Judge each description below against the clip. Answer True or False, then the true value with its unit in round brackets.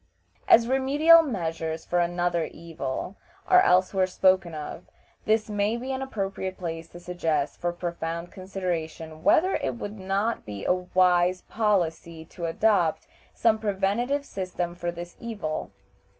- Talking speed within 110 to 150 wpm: True (135 wpm)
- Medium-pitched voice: True (180 Hz)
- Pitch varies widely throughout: False (3.9 semitones)